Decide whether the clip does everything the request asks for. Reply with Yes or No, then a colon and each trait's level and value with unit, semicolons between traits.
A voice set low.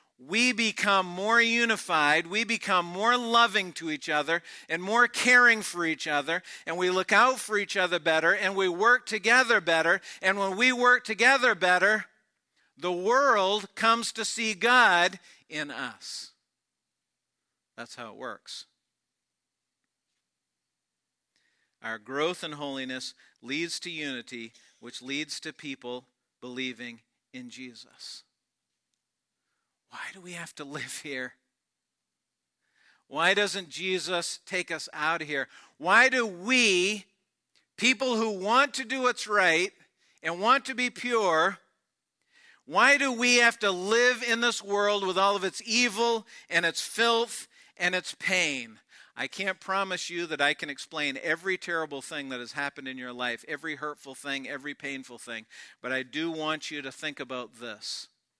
No: medium, 180 Hz